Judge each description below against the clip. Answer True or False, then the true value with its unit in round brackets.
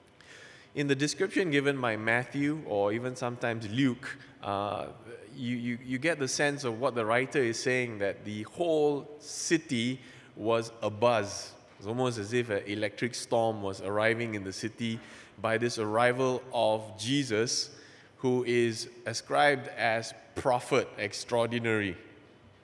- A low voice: True (120 Hz)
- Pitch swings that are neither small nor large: True (3.3 semitones)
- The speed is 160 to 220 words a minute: False (140 wpm)